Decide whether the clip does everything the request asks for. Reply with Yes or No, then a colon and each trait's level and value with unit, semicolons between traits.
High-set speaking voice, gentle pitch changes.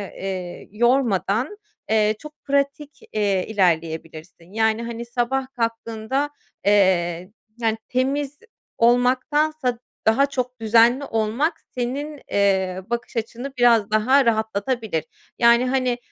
No: high, 235 Hz; average, 4.1 semitones